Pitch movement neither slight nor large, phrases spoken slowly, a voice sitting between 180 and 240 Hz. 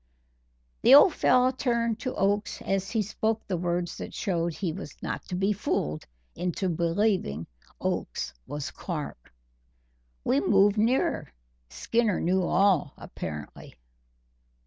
Yes: average, 4.4 semitones; slow, 125 wpm; high, 190 Hz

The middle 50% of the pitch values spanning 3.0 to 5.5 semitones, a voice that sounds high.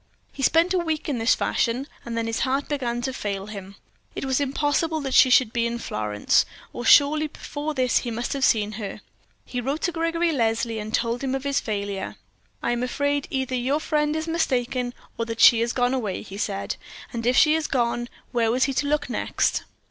Yes: average, 3.9 semitones; very high, 250 Hz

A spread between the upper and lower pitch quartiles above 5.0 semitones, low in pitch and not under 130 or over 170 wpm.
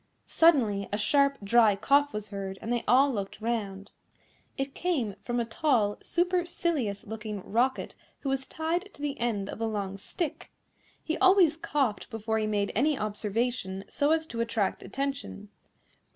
No: wide, 5.5 semitones; high, 235 Hz; average, 160 wpm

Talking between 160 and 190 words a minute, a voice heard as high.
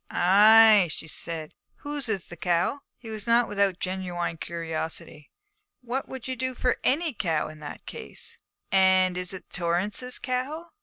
Yes: average, 165 wpm; high, 195 Hz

